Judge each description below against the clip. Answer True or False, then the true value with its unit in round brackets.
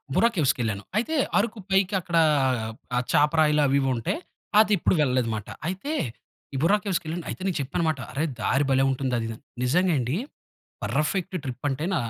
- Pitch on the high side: False (150 Hz)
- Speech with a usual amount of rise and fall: False (5.9 semitones)